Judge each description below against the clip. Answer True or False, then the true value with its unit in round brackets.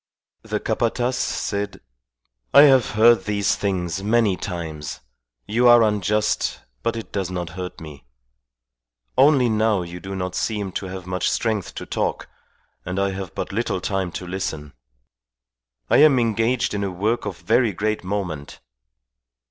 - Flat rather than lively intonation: False (3.7 semitones)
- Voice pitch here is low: True (100 Hz)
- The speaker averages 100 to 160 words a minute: True (150 wpm)